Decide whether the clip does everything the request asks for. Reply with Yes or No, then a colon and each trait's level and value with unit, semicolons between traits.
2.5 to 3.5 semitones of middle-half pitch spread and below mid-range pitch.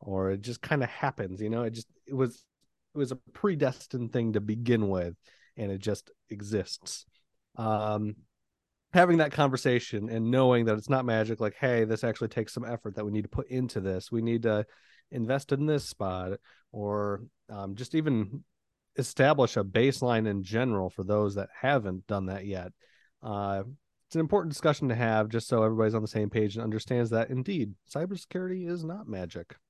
No: average, 3.9 semitones; low, 115 Hz